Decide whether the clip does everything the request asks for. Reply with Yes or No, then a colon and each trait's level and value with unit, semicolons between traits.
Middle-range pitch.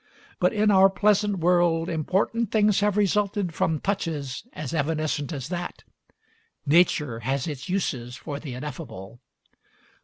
Yes: medium, 165 Hz